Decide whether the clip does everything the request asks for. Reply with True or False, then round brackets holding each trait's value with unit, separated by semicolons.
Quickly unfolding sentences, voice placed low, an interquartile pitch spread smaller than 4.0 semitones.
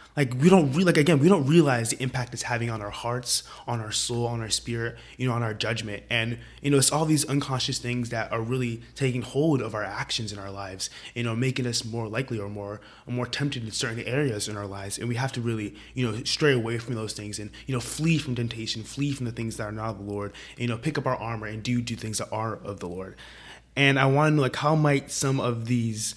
True (270 wpm; 120 Hz; 3.5 semitones)